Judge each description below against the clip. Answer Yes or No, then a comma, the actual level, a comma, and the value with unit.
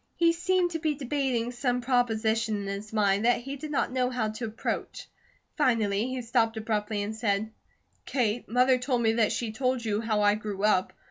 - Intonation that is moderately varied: Yes, average, 3.1 semitones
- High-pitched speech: Yes, high, 230 Hz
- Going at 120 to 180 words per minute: No, average, 195 wpm